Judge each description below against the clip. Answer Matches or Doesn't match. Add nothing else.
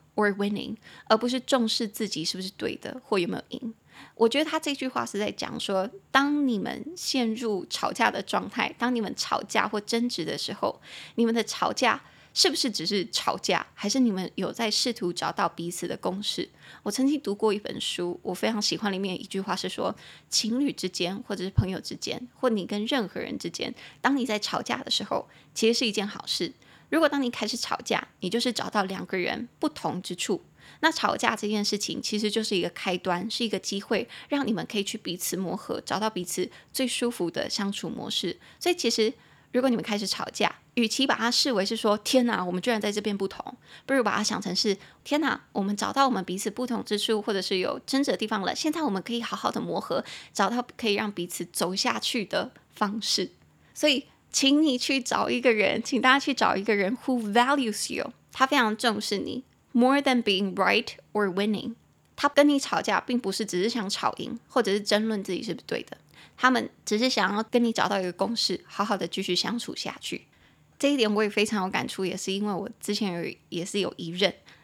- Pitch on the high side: Matches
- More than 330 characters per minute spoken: Matches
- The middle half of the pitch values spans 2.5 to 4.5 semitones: Matches